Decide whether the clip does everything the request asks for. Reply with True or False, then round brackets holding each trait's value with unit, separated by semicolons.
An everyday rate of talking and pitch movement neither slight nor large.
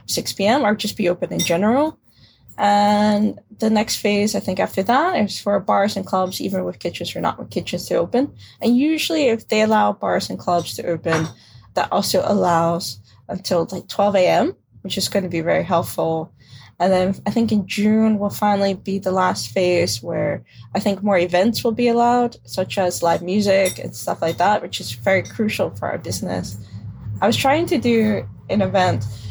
True (195 wpm; 3.6 semitones)